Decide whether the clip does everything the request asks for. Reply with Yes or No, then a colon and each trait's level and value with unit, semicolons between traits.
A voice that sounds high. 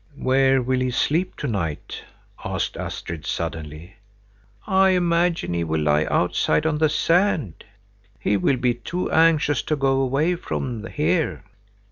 No: low, 135 Hz